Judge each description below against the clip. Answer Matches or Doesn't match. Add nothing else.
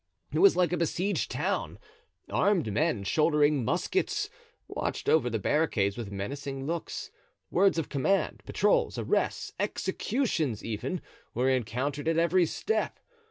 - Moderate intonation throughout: Doesn't match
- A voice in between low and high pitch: Matches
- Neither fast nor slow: Doesn't match